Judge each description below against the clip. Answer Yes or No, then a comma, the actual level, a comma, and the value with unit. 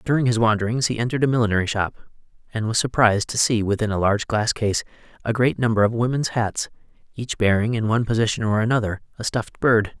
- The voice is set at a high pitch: No, low, 115 Hz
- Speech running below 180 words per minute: No, fast, 205 wpm